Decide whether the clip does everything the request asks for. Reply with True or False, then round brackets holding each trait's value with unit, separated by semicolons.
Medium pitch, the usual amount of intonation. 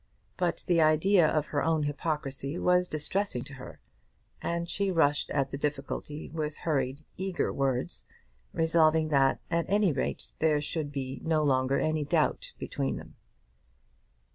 True (155 Hz; 3.1 semitones)